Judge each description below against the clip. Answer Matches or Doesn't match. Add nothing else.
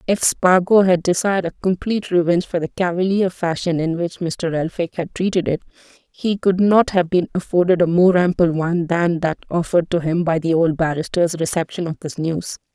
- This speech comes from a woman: Matches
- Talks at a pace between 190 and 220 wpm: Matches